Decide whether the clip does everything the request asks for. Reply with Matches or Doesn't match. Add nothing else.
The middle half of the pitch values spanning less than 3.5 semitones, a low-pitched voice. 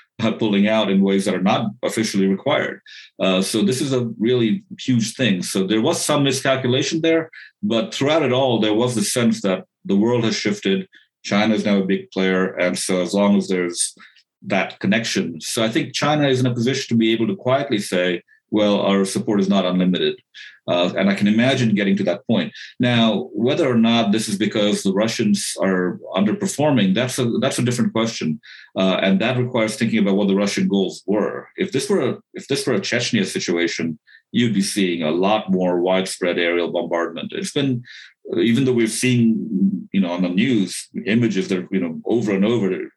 Doesn't match